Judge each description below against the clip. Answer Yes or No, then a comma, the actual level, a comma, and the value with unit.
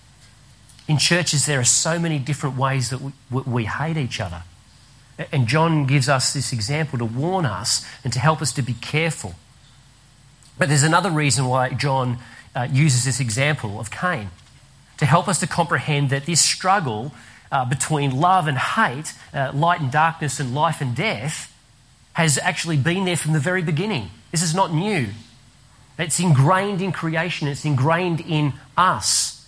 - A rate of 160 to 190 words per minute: Yes, average, 170 wpm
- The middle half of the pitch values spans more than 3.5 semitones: Yes, average, 4.2 semitones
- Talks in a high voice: No, medium, 140 Hz